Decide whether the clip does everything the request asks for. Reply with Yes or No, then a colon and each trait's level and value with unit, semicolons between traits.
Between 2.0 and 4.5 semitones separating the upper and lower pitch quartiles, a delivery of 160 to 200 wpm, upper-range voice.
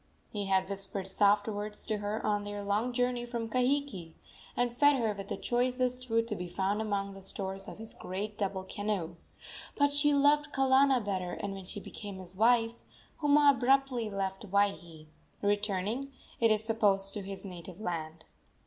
Yes: average, 4.0 semitones; average, 175 wpm; high, 205 Hz